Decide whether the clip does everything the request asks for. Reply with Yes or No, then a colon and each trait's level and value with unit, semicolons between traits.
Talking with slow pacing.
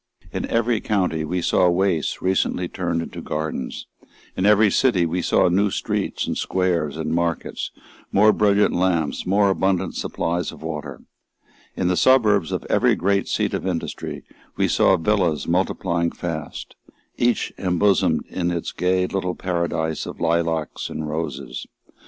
No: average, 145 wpm